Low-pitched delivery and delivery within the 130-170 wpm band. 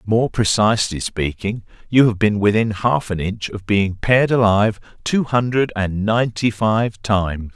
Yes: low, 105 Hz; average, 160 wpm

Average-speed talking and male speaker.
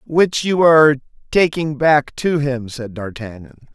Yes: average, 145 wpm; male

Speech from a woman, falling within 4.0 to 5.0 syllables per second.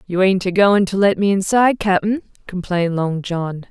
Yes: female; 4.8 syllables/s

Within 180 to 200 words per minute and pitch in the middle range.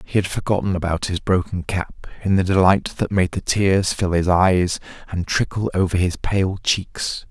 No: average, 190 wpm; very low, 90 Hz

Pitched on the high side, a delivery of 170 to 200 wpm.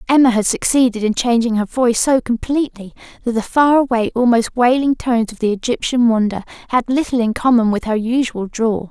Yes: high, 235 Hz; average, 190 wpm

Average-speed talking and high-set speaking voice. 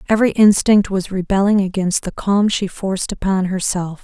Yes: average, 165 wpm; high, 195 Hz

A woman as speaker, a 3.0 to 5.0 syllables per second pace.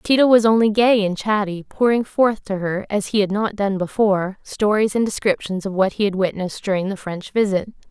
No: female; 5.5 syllables/s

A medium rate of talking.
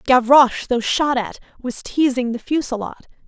Yes: average, 145 wpm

